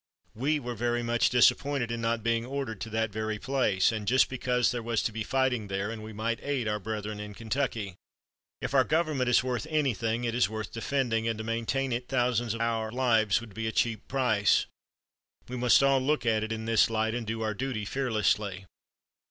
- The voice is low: Yes, low, 115 Hz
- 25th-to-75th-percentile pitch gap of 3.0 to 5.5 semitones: No, narrow, 2.5 semitones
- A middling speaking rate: No, fast, 210 wpm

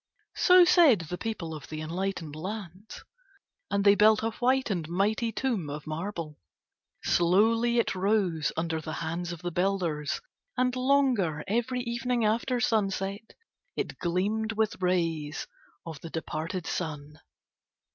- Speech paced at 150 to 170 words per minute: No, slow, 135 wpm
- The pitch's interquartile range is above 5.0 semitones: Yes, wide, 5.4 semitones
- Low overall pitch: No, high, 195 Hz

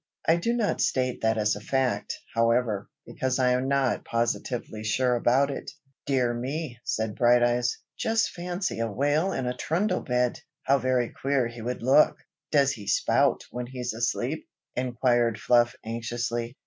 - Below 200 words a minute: Yes, average, 160 wpm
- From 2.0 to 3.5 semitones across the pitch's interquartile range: Yes, narrow, 2.6 semitones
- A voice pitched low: Yes, low, 125 Hz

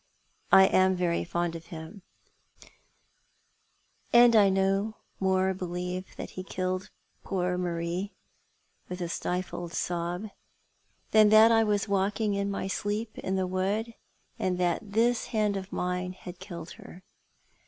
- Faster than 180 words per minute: No, average, 150 wpm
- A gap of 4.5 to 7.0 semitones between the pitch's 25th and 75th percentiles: No, narrow, 2.4 semitones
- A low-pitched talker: No, high, 190 Hz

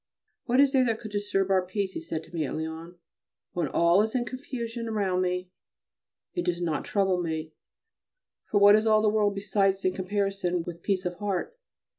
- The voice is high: Yes, high, 195 Hz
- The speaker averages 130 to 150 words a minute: No, average, 195 wpm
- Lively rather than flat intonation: No, average, 3.3 semitones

